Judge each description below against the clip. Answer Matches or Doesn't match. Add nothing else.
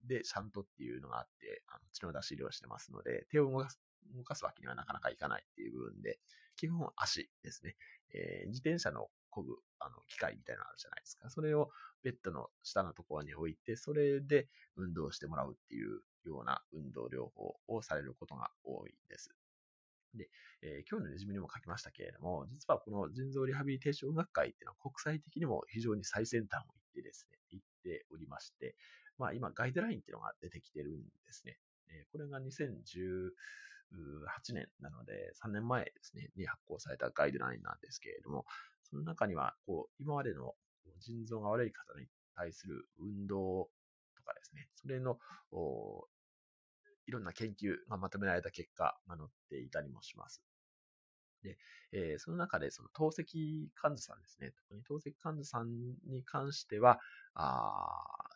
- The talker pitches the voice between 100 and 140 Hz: Matches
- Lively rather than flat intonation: Matches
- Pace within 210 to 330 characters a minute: Doesn't match